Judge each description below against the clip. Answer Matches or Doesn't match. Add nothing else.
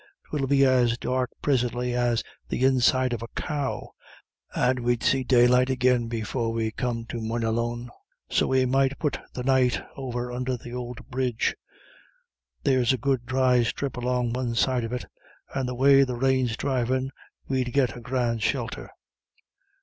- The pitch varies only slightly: Matches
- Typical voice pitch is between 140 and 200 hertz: Doesn't match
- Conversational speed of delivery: Matches